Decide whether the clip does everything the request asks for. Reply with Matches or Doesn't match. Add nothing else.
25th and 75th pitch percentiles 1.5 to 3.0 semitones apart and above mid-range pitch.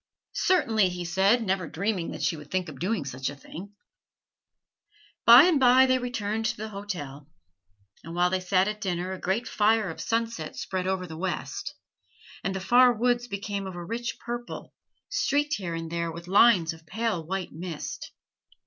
Doesn't match